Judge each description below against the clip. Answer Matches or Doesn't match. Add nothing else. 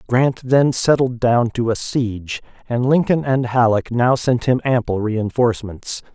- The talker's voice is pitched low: Matches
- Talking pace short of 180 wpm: Matches